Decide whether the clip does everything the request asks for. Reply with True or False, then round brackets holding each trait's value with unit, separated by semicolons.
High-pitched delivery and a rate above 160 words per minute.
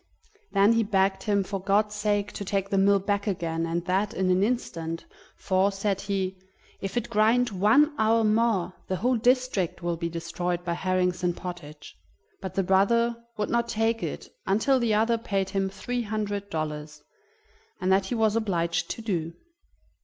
True (195 Hz; 175 wpm)